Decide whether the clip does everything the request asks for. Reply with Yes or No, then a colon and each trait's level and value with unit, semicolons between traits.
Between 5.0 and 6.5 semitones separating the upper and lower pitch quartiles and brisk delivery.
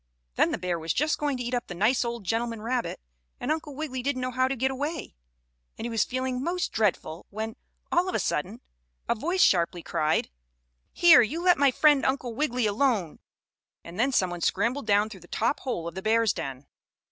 Yes: average, 5.3 semitones; fast, 210 wpm